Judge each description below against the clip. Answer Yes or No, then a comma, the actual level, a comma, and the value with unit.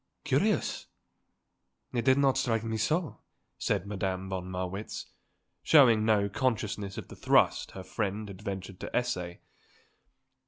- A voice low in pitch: Yes, low, 105 Hz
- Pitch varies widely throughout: No, average, 3.7 semitones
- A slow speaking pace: Yes, slow, 130 wpm